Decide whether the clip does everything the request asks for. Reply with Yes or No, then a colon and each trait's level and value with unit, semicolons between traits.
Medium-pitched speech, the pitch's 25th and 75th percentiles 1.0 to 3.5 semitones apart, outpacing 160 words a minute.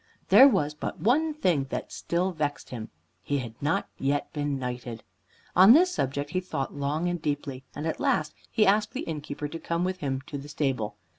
No: medium, 150 Hz; average, 4.6 semitones; average, 200 wpm